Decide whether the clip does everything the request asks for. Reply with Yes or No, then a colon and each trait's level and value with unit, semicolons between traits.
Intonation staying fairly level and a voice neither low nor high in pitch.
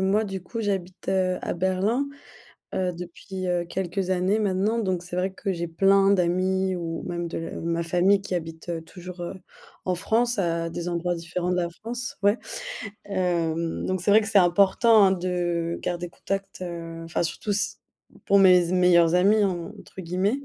Yes: narrow, 2.2 semitones; medium, 180 Hz